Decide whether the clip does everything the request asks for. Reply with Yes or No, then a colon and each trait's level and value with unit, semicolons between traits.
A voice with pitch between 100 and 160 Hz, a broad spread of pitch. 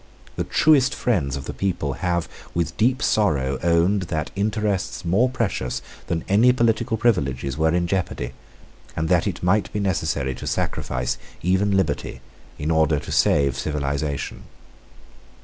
No: very low, 85 Hz; wide, 6.3 semitones